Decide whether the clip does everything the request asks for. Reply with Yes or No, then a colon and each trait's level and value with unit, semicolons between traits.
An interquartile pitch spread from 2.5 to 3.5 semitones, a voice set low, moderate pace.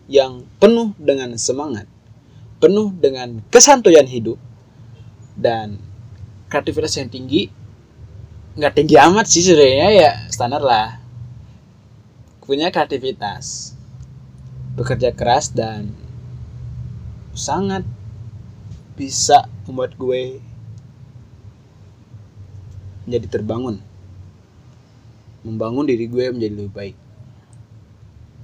No: average, 2.9 semitones; low, 120 Hz; slow, 80 wpm